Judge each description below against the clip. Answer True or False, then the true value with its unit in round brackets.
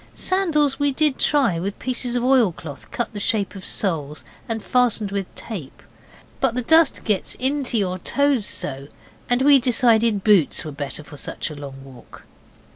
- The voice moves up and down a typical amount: False (7.3 semitones)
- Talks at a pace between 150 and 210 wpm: True (175 wpm)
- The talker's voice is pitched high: True (225 Hz)